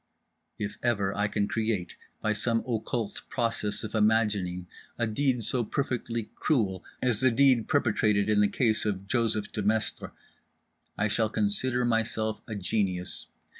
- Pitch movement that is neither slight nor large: No, narrow, 2.2 semitones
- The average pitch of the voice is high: No, low, 110 Hz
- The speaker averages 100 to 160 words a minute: Yes, average, 140 wpm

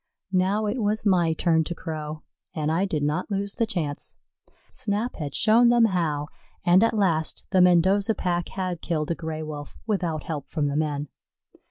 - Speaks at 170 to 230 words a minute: Yes, average, 180 wpm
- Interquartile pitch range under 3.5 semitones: No, average, 4.5 semitones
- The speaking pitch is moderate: Yes, medium, 175 Hz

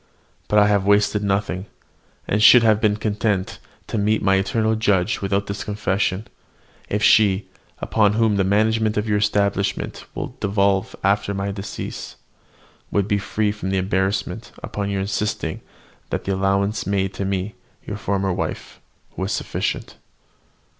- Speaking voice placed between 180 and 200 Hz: No, low, 100 Hz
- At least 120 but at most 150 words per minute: Yes, average, 145 wpm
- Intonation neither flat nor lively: No, narrow, 1.4 semitones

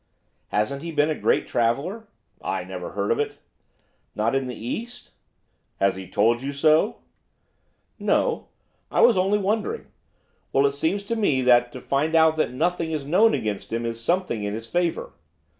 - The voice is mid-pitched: Yes, medium, 150 Hz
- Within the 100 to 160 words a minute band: No, average, 175 wpm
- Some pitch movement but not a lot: No, wide, 7.7 semitones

